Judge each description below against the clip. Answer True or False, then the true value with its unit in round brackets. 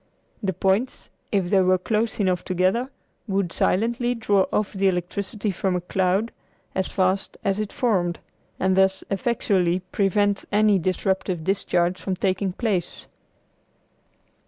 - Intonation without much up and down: True (2.0 semitones)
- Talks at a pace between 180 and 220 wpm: False (135 wpm)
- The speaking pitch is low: False (190 Hz)